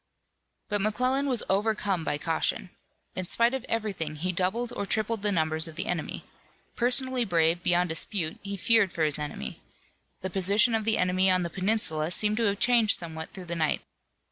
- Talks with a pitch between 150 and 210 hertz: Yes, high, 190 Hz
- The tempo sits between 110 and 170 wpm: No, average, 185 wpm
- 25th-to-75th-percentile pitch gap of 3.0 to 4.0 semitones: No, average, 4.8 semitones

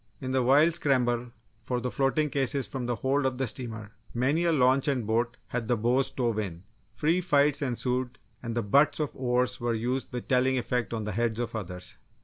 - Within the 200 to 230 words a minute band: Yes, fast, 205 wpm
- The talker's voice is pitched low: Yes, low, 125 Hz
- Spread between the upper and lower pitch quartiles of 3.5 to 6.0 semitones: No, narrow, 2.5 semitones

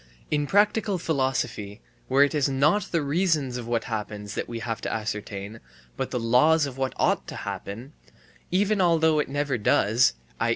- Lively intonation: Yes, wide, 5.8 semitones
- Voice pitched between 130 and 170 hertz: Yes, low, 135 Hz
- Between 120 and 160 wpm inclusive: No, average, 180 wpm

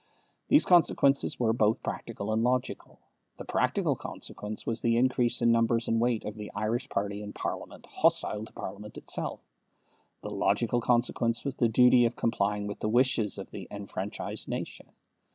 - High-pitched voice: No, low, 115 Hz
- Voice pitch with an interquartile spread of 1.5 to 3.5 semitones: Yes, narrow, 2.5 semitones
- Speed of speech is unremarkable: Yes, average, 165 wpm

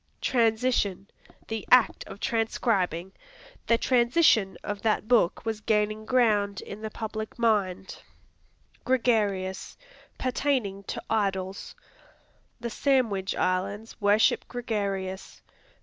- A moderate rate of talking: No, slow, 100 wpm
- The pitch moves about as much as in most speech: Yes, average, 3.1 semitones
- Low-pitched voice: No, high, 215 Hz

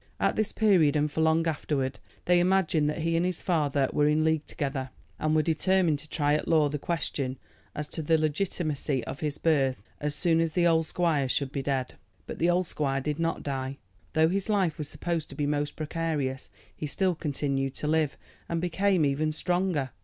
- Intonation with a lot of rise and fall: No, narrow, 2.6 semitones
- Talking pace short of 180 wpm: No, fast, 205 wpm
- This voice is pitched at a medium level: Yes, medium, 155 Hz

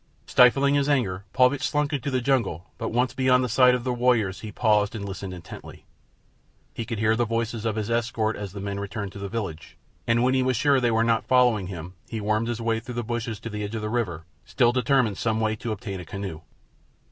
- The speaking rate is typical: No, fast, 240 wpm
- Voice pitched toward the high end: No, low, 115 Hz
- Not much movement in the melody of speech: No, average, 3.4 semitones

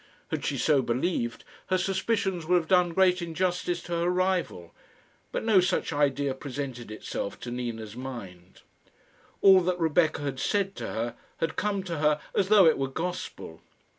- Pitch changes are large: Yes, wide, 5.9 semitones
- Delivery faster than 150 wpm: Yes, average, 165 wpm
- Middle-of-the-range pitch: Yes, medium, 165 Hz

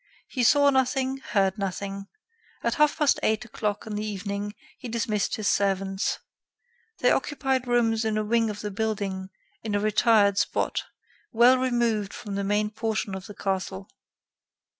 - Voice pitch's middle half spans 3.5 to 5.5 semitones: No, average, 3.0 semitones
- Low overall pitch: No, high, 215 Hz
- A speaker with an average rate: Yes, average, 160 wpm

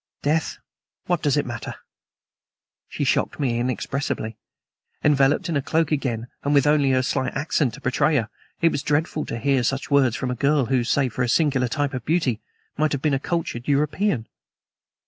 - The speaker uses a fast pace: No, average, 185 wpm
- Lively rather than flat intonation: No, average, 3.0 semitones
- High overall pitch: No, medium, 140 Hz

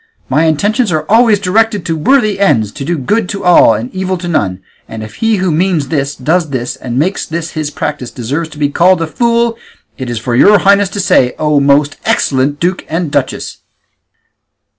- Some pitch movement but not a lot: No, wide, 5.8 semitones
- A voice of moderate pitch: Yes, medium, 160 Hz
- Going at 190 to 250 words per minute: Yes, average, 200 wpm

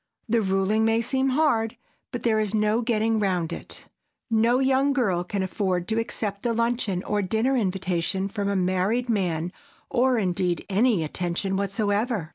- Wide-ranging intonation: No, average, 3.7 semitones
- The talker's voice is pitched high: Yes, high, 210 Hz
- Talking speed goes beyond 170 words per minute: No, average, 160 wpm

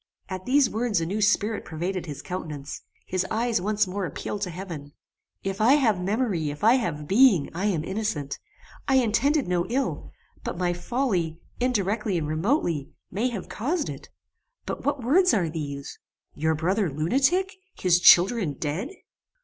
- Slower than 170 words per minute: Yes, average, 160 wpm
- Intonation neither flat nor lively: No, wide, 6.2 semitones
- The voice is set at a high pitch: Yes, high, 195 Hz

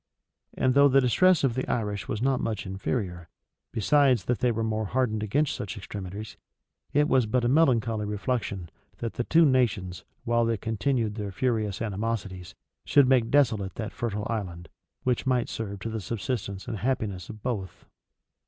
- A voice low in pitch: Yes, low, 115 Hz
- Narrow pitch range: No, average, 3.9 semitones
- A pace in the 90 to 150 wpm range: No, average, 170 wpm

